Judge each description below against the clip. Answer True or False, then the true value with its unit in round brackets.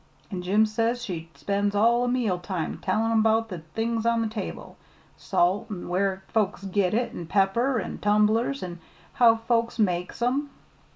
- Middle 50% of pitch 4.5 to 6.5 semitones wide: False (3.4 semitones)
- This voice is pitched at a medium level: False (215 Hz)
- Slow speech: False (170 wpm)